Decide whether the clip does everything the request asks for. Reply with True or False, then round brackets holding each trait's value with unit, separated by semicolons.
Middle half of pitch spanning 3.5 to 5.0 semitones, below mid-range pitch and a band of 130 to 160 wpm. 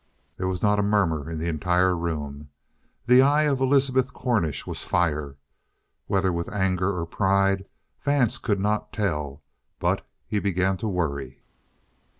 True (4.3 semitones; 95 Hz; 150 wpm)